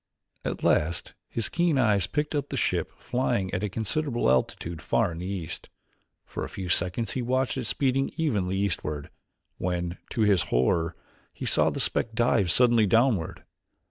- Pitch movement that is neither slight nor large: No, wide, 6.2 semitones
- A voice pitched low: Yes, low, 105 Hz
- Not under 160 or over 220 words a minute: Yes, average, 170 wpm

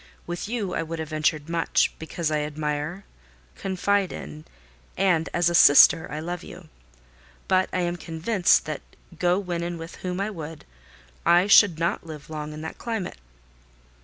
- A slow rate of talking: No, average, 165 wpm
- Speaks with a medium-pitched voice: Yes, medium, 170 Hz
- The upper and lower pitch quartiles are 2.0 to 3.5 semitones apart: Yes, average, 2.8 semitones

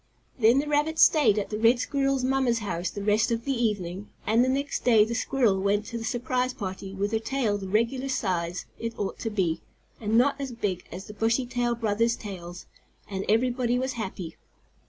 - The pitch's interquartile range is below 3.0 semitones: No, average, 3.8 semitones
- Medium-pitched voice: No, high, 225 Hz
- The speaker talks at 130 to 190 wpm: No, average, 200 wpm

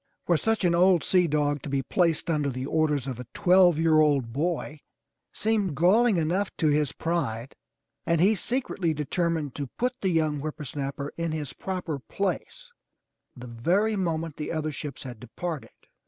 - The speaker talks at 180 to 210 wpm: No, average, 170 wpm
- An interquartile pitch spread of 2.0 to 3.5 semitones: No, average, 3.9 semitones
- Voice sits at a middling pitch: Yes, medium, 160 Hz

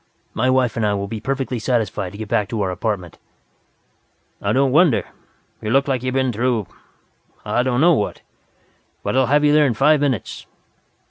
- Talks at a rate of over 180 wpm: Yes, average, 190 wpm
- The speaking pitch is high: No, low, 125 Hz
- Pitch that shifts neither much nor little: Yes, average, 4.1 semitones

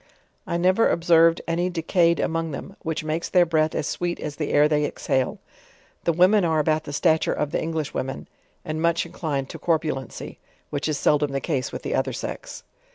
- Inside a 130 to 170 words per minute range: No, average, 195 wpm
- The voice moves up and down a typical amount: No, narrow, 2.2 semitones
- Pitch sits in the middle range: Yes, medium, 160 Hz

